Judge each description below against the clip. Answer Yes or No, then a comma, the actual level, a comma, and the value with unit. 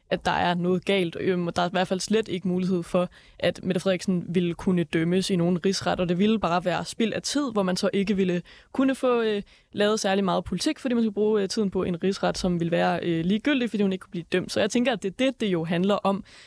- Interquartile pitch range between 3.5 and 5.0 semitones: No, average, 2.8 semitones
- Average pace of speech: No, fast, 260 wpm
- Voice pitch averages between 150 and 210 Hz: Yes, high, 190 Hz